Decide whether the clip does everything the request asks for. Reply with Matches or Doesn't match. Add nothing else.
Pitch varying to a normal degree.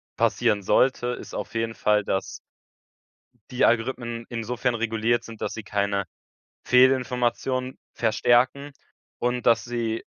Doesn't match